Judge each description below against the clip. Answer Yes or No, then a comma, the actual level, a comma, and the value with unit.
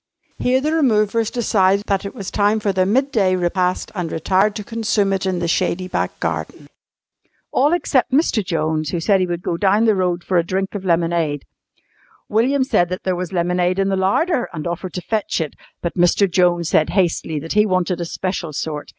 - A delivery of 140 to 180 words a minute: No, average, 200 wpm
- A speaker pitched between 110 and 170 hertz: No, medium, 185 Hz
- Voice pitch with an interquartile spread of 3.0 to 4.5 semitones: Yes, average, 3.3 semitones